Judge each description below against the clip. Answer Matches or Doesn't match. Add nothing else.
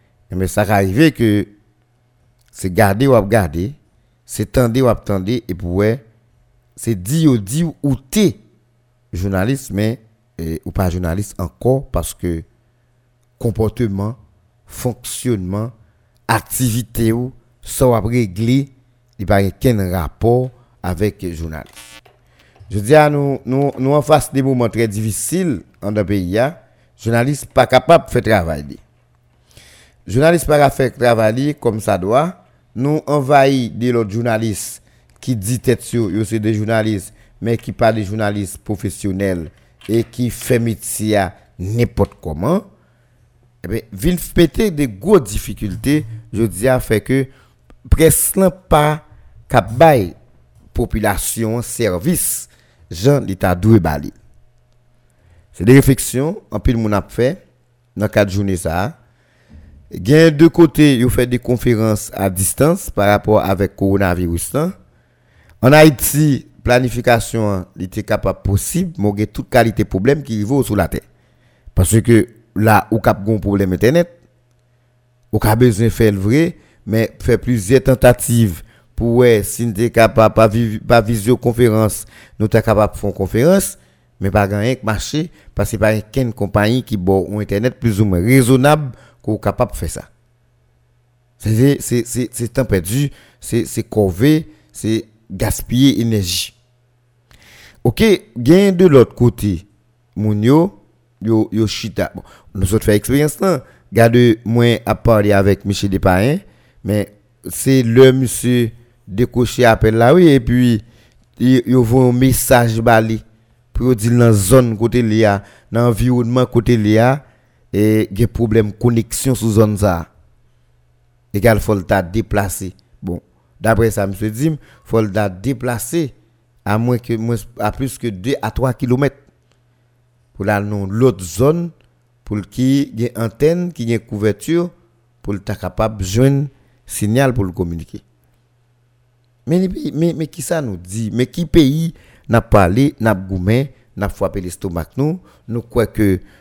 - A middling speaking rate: Doesn't match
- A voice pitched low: Matches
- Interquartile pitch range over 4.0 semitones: Doesn't match